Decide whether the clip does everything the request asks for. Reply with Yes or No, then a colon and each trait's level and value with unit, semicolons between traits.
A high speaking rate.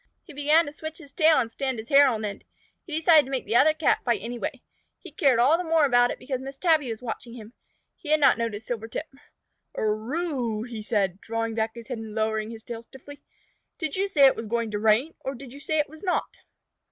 Yes: fast, 240 wpm